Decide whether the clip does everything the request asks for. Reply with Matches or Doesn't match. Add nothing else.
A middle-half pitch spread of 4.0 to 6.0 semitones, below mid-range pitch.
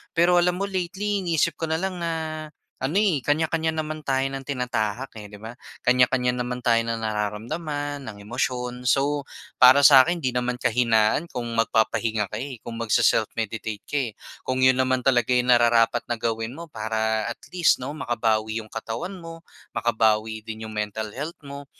Matches